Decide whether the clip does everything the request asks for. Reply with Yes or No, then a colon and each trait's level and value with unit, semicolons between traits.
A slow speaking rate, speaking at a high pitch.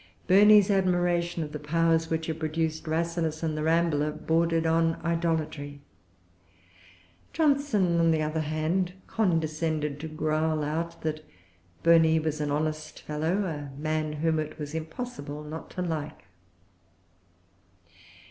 No: slow, 130 wpm; medium, 160 Hz